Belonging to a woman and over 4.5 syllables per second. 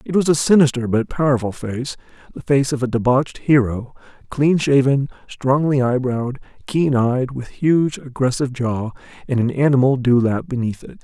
No: male; 5.0 syllables/s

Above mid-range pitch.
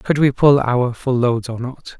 No: low, 125 Hz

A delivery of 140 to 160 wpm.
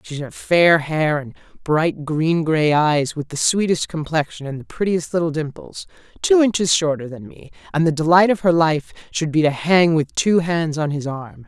No: fast, 205 wpm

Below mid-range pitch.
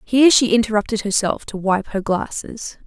No: high, 215 Hz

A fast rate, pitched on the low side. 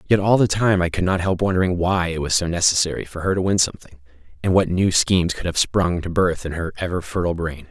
Yes: fast, 255 wpm; very low, 90 Hz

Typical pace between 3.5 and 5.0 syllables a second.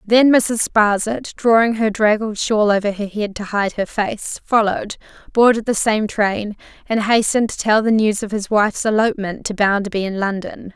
Yes: 4.9 syllables/s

